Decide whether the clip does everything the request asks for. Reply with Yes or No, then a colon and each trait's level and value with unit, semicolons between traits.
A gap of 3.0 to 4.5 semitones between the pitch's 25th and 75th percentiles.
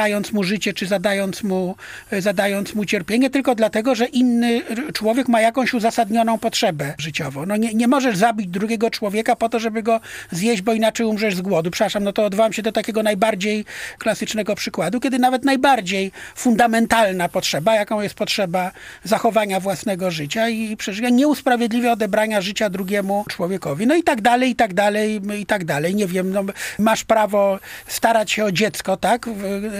No: narrow, 2.5 semitones